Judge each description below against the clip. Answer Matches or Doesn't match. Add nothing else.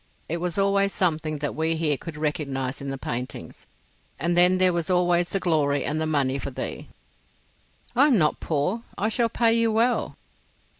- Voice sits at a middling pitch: Matches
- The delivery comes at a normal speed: Matches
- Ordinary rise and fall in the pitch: Matches